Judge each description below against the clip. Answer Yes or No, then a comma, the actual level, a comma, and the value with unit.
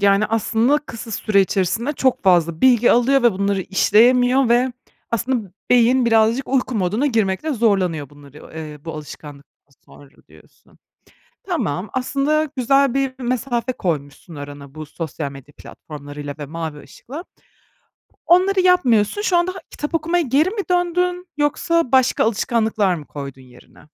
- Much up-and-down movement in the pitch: Yes, wide, 8.7 semitones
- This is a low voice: No, high, 225 Hz